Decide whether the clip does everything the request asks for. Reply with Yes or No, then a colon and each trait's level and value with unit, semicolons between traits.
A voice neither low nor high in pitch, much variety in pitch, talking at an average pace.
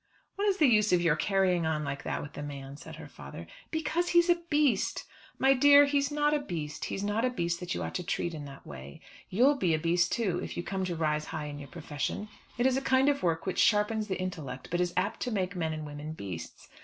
No: medium, 180 Hz; wide, 8.7 semitones; fast, 255 wpm